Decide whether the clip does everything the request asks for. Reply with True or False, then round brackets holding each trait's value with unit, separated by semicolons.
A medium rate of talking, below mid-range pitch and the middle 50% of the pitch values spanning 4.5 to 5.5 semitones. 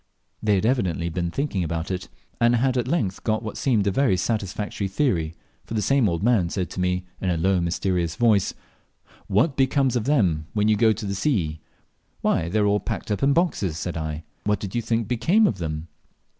False (215 wpm; 100 Hz; 5.0 semitones)